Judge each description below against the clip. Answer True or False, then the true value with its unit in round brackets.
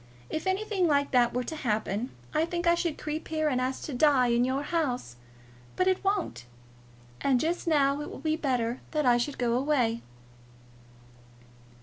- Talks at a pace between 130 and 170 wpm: False (180 wpm)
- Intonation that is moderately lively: True (4.4 semitones)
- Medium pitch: False (285 Hz)